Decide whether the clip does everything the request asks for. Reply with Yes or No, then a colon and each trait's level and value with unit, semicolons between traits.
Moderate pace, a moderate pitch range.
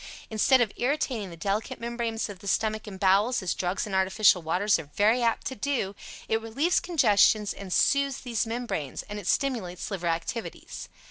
Yes: average, 180 wpm; average, 3.9 semitones